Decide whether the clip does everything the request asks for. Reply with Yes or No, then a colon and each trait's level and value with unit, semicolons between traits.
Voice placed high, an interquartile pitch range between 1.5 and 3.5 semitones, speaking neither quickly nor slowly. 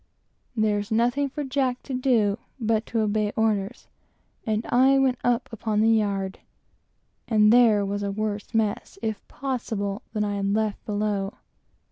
Yes: high, 215 Hz; average, 2.8 semitones; average, 150 wpm